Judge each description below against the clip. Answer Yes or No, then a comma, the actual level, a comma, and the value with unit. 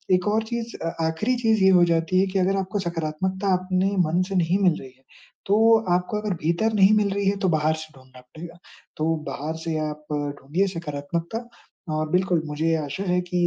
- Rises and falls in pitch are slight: No, average, 3.8 semitones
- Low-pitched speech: No, medium, 180 Hz